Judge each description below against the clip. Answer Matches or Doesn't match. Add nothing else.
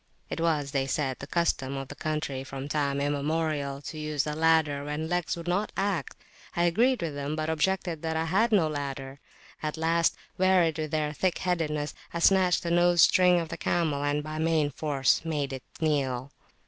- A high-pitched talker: Doesn't match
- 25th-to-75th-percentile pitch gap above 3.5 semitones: Doesn't match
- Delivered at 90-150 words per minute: Doesn't match